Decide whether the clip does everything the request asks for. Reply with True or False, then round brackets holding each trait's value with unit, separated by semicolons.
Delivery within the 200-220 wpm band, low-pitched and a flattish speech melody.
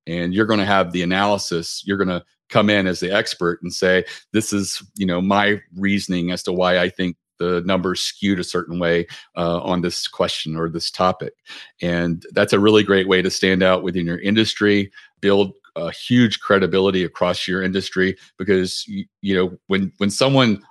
False (190 wpm; 95 Hz; 2.1 semitones)